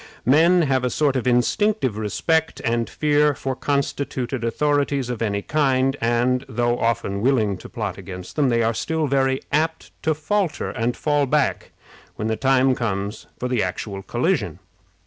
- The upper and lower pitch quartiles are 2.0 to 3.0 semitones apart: No, average, 4.1 semitones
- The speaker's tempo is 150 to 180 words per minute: Yes, average, 160 wpm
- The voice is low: Yes, low, 130 Hz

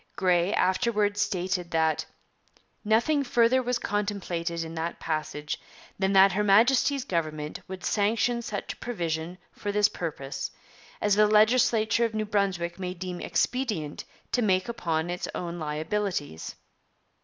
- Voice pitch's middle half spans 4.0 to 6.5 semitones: Yes, average, 4.3 semitones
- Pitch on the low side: No, high, 195 Hz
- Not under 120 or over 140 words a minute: Yes, slow, 135 wpm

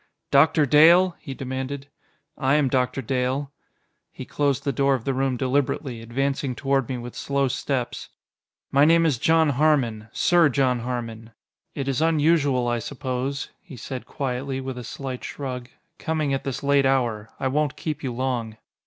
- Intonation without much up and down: Yes, narrow, 2.2 semitones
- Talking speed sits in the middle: Yes, average, 165 wpm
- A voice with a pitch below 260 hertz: Yes, low, 135 Hz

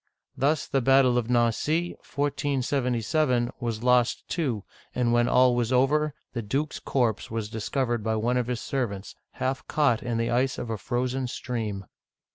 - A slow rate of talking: No, average, 165 wpm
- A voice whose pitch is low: Yes, low, 125 Hz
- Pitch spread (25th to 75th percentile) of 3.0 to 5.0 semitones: No, narrow, 2.5 semitones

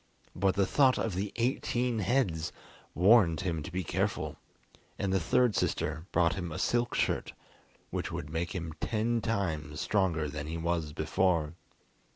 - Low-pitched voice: Yes, very low, 90 Hz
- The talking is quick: No, average, 160 wpm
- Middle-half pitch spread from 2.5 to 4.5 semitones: No, average, 5.2 semitones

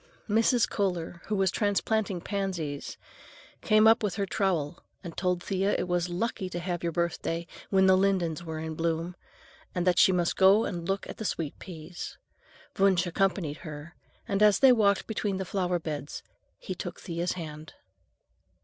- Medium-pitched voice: Yes, medium, 180 Hz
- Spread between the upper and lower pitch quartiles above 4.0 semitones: No, average, 2.8 semitones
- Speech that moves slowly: No, average, 170 wpm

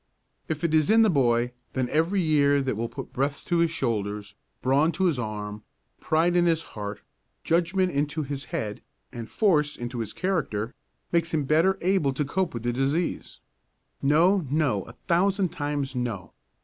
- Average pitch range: No, wide, 5.8 semitones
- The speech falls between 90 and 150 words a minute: No, average, 175 wpm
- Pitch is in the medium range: Yes, medium, 145 Hz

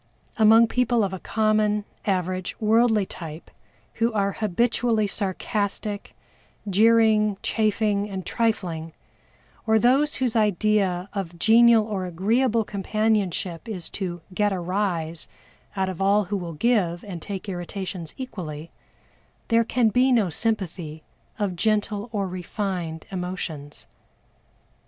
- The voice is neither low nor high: No, high, 205 Hz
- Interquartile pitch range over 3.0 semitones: Yes, average, 3.4 semitones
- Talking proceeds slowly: Yes, slow, 120 wpm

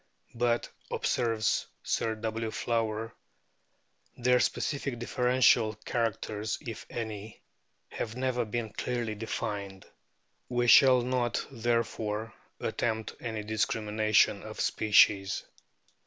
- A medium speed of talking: No, slow, 100 wpm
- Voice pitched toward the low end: Yes, low, 115 Hz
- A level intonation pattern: Yes, narrow, 1.9 semitones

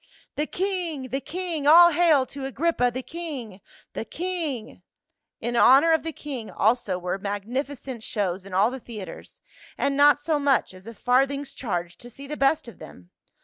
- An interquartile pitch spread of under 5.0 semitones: No, average, 5.3 semitones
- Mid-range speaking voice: No, very high, 270 Hz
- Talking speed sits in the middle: Yes, average, 190 wpm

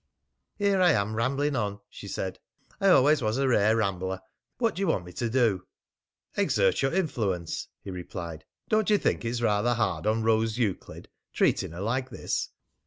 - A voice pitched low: Yes, low, 115 Hz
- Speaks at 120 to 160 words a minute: No, average, 175 wpm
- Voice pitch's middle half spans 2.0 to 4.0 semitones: No, wide, 5.4 semitones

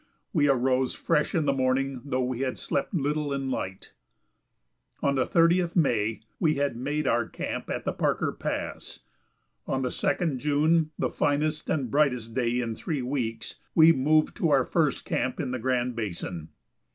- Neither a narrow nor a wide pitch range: Yes, average, 3.3 semitones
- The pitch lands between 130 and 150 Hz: Yes, low, 135 Hz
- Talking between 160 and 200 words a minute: Yes, average, 170 wpm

